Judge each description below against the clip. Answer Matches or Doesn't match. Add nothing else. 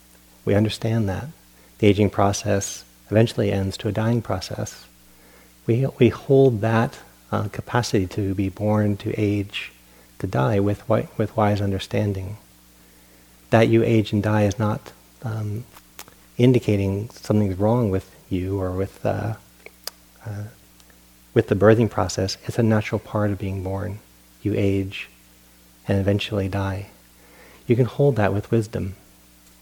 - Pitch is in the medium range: Doesn't match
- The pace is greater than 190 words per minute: Doesn't match